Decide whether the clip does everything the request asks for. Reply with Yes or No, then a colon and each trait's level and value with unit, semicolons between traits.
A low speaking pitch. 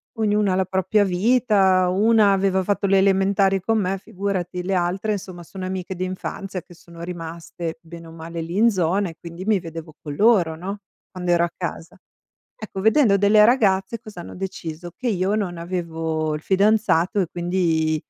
No: medium, 185 Hz